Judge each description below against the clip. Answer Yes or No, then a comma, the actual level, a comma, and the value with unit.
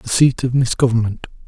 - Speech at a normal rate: Yes, average, 160 wpm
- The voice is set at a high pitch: No, low, 125 Hz